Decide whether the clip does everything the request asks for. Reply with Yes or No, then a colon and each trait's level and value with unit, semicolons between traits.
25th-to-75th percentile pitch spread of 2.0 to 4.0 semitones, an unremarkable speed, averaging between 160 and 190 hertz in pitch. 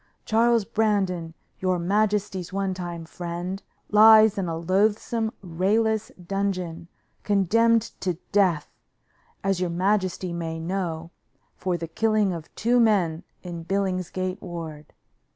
No: average, 3.5 semitones; slow, 115 wpm; medium, 185 Hz